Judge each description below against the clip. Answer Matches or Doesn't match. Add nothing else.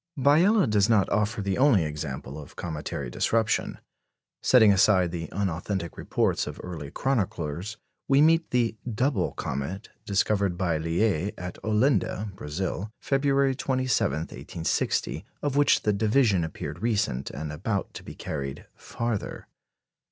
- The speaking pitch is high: Doesn't match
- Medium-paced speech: Doesn't match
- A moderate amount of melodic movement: Doesn't match